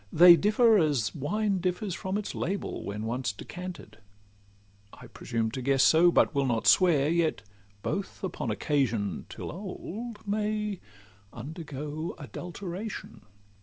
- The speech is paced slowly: Yes, slow, 125 wpm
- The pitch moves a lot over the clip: Yes, wide, 8.5 semitones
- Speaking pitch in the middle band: Yes, medium, 160 Hz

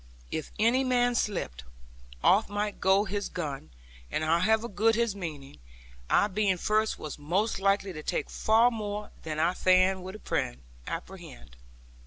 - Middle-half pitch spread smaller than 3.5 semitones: No, average, 4.3 semitones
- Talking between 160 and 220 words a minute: No, average, 145 wpm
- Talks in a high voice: Yes, high, 195 Hz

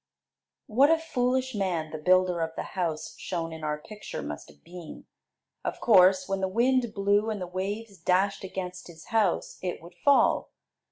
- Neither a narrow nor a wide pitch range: Yes, average, 3.9 semitones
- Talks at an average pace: Yes, average, 175 wpm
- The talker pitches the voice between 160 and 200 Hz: Yes, medium, 185 Hz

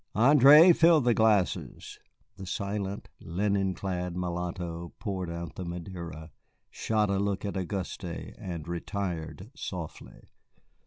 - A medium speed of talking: No, slow, 115 wpm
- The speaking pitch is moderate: No, very low, 95 Hz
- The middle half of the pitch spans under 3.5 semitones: Yes, average, 3.0 semitones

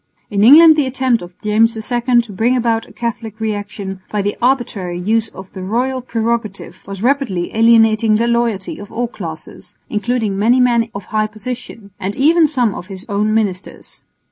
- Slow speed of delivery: No, average, 175 wpm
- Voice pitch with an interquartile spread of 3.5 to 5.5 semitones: No, average, 3.0 semitones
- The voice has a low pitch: No, high, 225 Hz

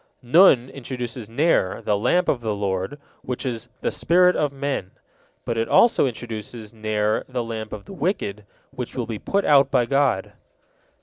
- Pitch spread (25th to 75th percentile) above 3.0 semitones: Yes, average, 4.5 semitones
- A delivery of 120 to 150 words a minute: No, average, 170 wpm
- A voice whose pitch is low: Yes, low, 120 Hz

